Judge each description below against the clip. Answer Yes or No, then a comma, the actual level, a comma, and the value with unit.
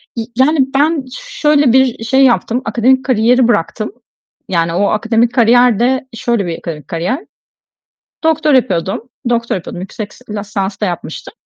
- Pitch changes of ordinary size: Yes, average, 4.6 semitones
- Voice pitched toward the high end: Yes, high, 235 Hz